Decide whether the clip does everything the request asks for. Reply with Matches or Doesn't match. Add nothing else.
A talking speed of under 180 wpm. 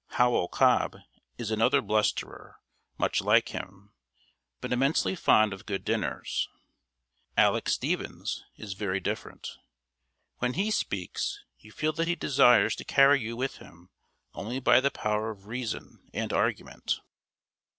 Matches